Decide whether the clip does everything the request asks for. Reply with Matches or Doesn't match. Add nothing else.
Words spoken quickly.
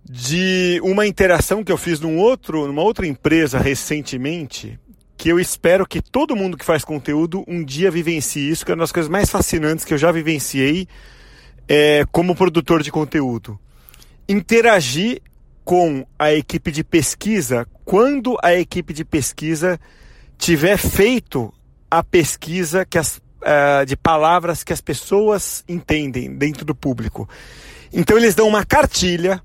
Doesn't match